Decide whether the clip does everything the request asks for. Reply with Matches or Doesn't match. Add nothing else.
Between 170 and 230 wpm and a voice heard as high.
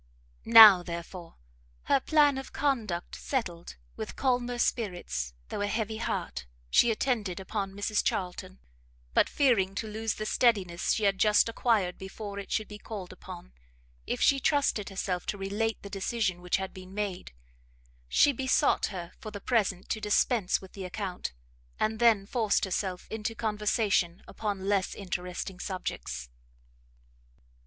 Doesn't match